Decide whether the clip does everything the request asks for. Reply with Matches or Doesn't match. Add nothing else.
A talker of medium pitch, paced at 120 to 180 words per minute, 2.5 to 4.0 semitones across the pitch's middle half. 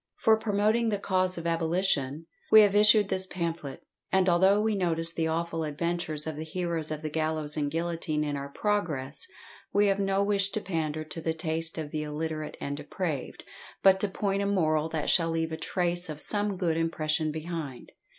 Doesn't match